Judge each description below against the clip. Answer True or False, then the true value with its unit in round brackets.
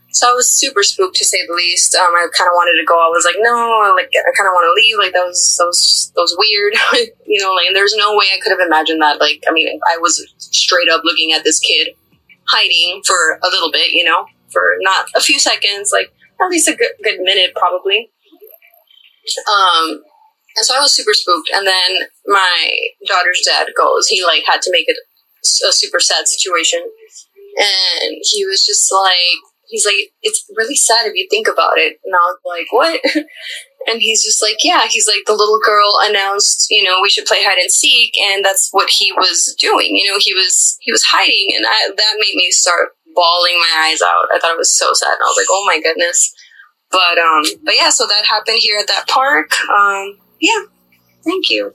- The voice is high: True (225 Hz)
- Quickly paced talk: True (220 wpm)